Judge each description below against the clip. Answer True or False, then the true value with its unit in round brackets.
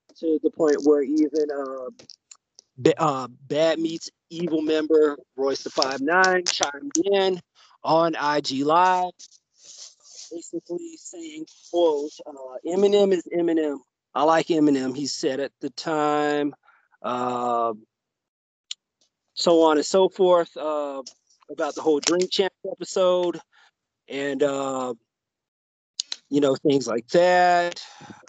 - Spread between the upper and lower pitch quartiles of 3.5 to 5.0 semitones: True (4.0 semitones)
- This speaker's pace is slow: True (115 wpm)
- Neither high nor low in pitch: True (155 Hz)